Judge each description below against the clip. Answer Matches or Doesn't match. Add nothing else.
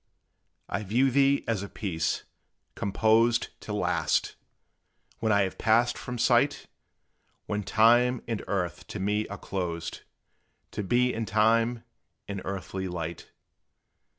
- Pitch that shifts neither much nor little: Matches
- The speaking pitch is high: Doesn't match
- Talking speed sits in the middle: Doesn't match